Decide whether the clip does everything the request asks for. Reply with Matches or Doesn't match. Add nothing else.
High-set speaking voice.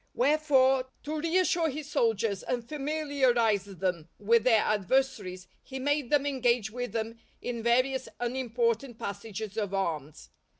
Matches